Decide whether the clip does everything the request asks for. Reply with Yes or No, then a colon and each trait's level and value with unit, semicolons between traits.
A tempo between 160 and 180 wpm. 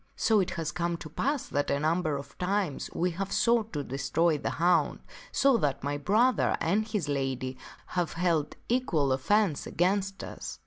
Yes: average, 175 wpm